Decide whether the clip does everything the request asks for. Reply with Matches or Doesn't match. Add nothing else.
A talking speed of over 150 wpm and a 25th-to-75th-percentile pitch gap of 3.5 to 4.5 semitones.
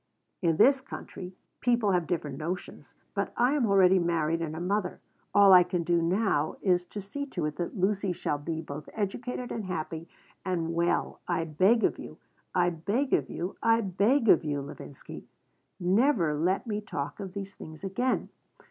Matches